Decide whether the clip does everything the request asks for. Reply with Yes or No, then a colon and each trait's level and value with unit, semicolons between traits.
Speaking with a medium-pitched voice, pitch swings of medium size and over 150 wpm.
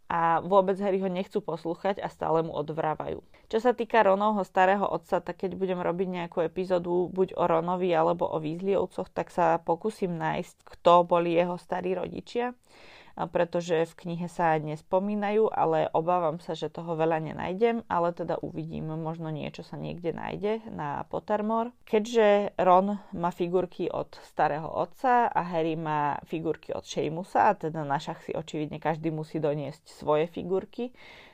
Yes: medium, 175 Hz; average, 3.3 semitones; average, 160 wpm